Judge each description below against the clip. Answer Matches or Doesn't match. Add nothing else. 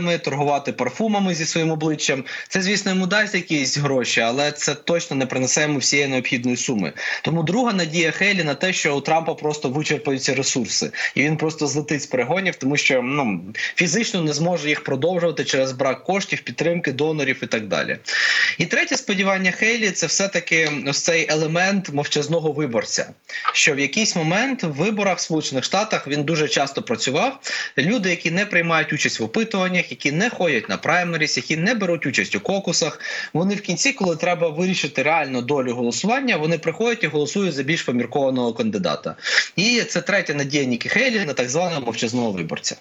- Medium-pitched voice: Matches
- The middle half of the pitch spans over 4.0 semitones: Matches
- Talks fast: Matches